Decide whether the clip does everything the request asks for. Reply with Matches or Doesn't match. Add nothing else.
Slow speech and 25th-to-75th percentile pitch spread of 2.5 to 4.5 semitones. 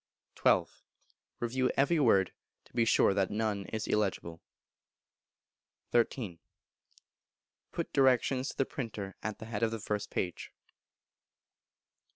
Matches